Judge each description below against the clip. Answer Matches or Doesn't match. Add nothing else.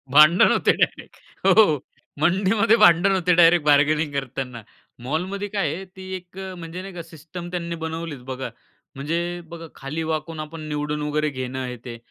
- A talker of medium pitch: Matches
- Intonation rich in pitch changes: Doesn't match